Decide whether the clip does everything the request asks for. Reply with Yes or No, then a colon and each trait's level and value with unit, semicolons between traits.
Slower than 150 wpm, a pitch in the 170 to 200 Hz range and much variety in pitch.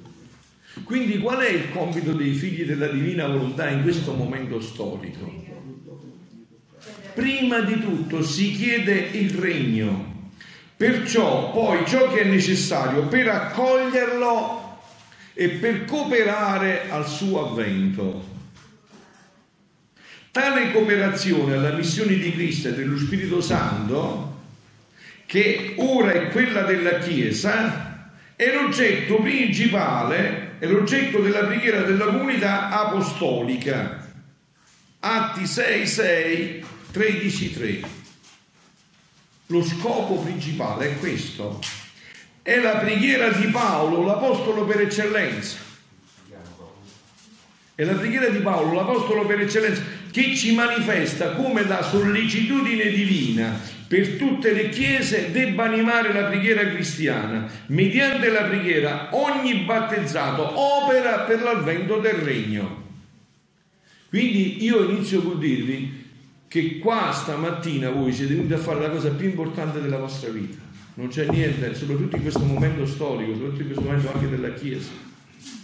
Yes: slow, 115 wpm; high, 190 Hz; wide, 6.2 semitones